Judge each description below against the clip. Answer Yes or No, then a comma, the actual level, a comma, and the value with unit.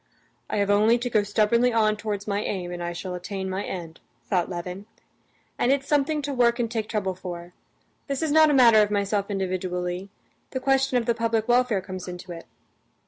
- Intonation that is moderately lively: Yes, average, 4.4 semitones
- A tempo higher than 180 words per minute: Yes, average, 200 wpm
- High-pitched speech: Yes, high, 210 Hz